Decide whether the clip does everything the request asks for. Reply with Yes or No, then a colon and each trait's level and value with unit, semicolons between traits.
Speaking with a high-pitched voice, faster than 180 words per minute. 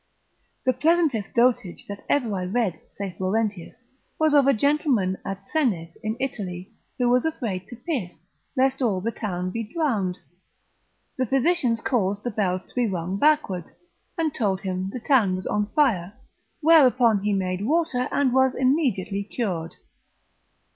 No: high, 225 Hz; average, 155 wpm